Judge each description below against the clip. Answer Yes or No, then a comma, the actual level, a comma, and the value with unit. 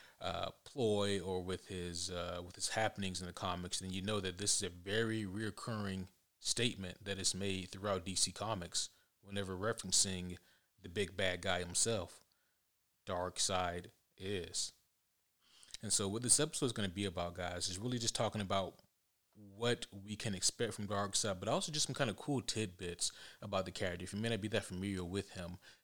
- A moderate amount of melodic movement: Yes, average, 3.0 semitones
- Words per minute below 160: No, average, 185 wpm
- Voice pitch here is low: Yes, low, 100 Hz